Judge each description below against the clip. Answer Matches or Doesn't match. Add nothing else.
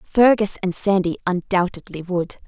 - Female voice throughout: Matches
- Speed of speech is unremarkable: Doesn't match